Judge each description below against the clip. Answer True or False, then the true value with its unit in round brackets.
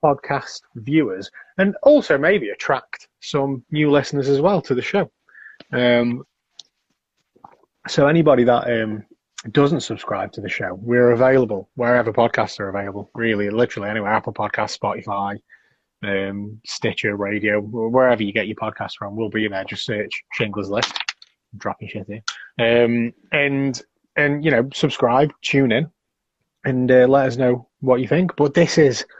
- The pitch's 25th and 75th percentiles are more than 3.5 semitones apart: True (4.5 semitones)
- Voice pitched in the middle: False (120 Hz)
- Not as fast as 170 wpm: True (155 wpm)